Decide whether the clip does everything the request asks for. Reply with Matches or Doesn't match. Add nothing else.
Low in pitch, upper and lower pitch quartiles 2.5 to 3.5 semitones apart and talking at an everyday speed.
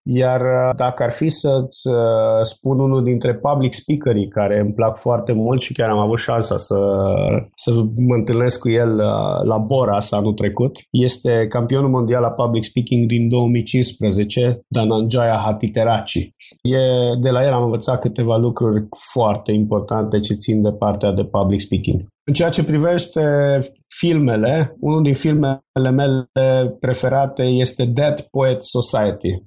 Matches